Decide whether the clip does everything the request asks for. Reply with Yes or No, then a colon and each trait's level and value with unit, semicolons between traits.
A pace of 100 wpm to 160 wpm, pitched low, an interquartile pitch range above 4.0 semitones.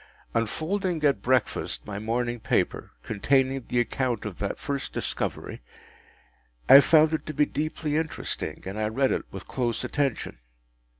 Yes: average, 145 wpm; low, 130 Hz; average, 4.7 semitones